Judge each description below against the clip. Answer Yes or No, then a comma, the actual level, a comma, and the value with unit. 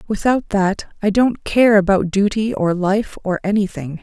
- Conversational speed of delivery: Yes, average, 165 wpm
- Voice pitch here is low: No, high, 200 Hz